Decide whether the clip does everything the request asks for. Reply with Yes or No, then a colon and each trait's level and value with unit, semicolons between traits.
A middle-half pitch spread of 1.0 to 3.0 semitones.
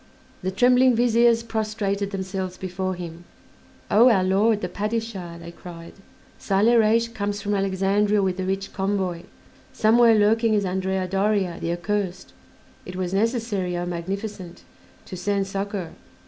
Yes: average, 2.7 semitones